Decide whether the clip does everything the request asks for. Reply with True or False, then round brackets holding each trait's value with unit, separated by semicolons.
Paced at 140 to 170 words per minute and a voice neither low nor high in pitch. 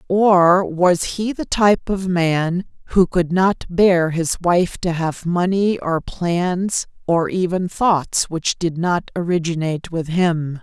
True (150 wpm; 175 Hz)